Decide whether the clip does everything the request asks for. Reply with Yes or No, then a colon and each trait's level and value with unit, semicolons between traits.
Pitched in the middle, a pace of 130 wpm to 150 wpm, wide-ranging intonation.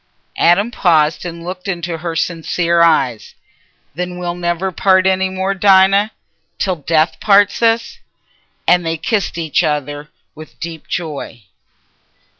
No: medium, 175 Hz; slow, 135 wpm; average, 2.7 semitones